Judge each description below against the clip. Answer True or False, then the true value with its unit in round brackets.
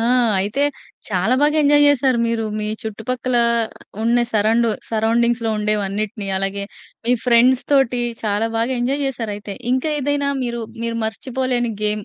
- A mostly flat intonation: False (3.2 semitones)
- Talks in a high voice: True (235 Hz)